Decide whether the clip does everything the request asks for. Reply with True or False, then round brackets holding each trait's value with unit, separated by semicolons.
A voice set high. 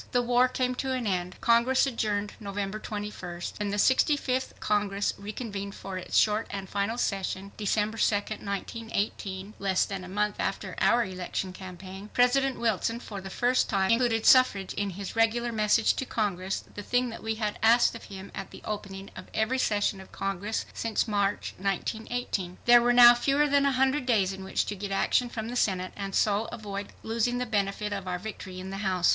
True (210 Hz)